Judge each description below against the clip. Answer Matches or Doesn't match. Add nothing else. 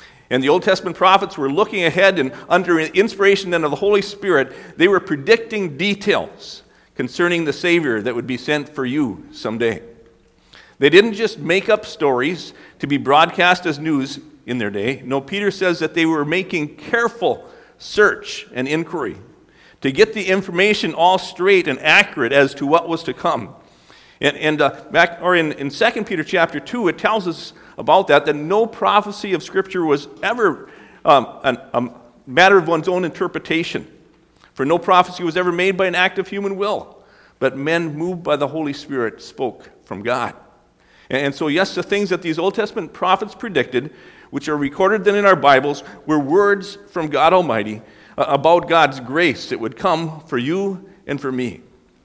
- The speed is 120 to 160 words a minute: Doesn't match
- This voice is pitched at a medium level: Matches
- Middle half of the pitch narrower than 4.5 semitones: Doesn't match